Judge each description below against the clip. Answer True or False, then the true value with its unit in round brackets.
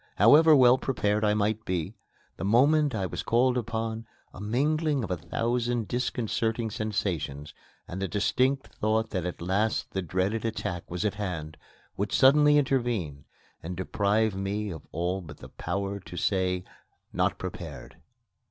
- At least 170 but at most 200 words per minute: False (150 wpm)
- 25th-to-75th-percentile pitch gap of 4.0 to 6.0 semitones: True (4.5 semitones)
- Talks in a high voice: False (105 Hz)